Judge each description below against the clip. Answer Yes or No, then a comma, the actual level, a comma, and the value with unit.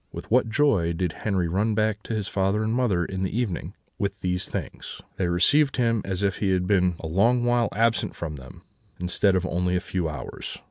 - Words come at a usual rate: No, fast, 215 wpm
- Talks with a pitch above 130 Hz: No, very low, 95 Hz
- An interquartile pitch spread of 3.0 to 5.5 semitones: Yes, average, 3.7 semitones